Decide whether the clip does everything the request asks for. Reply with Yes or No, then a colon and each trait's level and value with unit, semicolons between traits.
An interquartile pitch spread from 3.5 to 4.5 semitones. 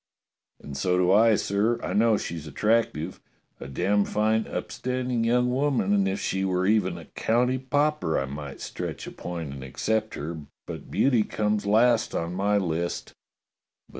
No: average, 4.9 semitones